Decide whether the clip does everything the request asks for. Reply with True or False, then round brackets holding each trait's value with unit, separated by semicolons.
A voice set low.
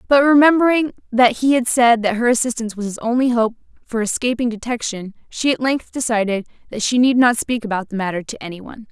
False (235 Hz)